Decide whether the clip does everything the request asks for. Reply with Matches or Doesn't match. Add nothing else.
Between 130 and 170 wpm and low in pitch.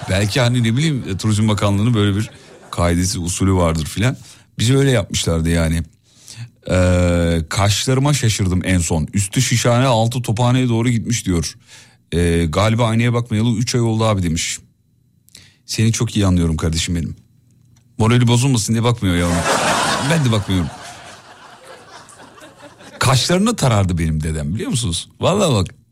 Matches